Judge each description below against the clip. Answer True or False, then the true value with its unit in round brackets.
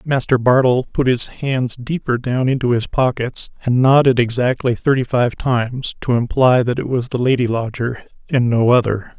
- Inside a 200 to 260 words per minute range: False (175 wpm)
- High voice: False (125 Hz)